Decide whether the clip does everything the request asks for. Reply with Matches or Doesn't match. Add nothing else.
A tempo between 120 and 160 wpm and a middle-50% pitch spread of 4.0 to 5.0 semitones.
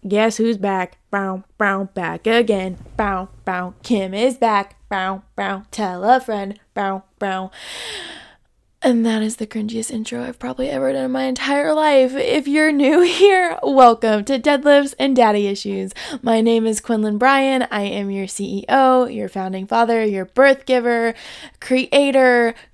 Matches